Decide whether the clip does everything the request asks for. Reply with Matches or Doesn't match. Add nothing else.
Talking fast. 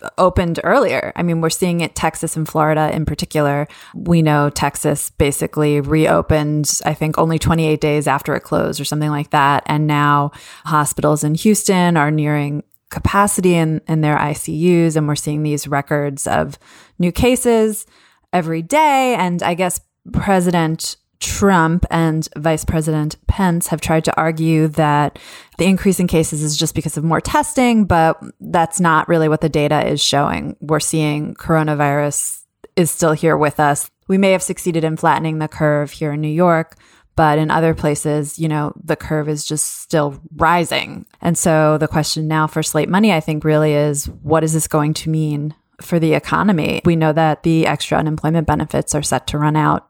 Doesn't match